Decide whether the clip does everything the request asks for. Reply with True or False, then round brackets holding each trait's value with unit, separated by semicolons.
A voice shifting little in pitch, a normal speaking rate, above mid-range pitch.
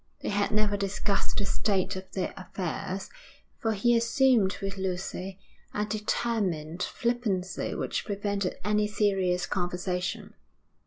False (2.3 semitones; 120 wpm; 200 Hz)